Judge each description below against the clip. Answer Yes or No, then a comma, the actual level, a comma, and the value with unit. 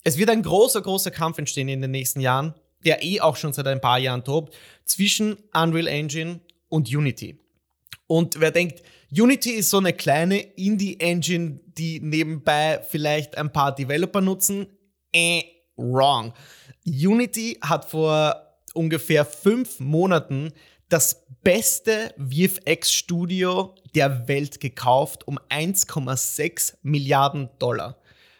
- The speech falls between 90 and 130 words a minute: Yes, slow, 125 wpm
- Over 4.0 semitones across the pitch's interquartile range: Yes, average, 4.4 semitones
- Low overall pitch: No, medium, 160 Hz